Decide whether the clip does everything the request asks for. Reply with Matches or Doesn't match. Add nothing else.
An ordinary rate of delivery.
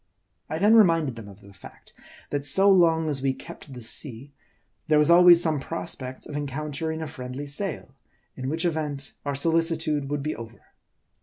Matches